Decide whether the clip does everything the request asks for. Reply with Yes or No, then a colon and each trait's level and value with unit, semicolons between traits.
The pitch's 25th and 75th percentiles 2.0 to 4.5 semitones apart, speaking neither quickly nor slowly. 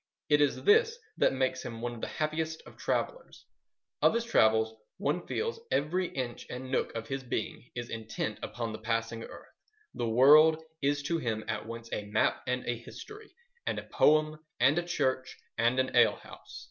No: average, 5.0 semitones; average, 185 wpm